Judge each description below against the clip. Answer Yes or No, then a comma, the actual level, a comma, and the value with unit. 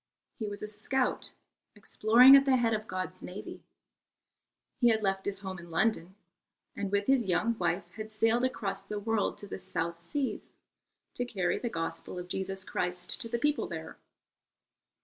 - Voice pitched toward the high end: Yes, high, 210 Hz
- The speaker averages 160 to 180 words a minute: Yes, average, 170 wpm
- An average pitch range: Yes, average, 3.7 semitones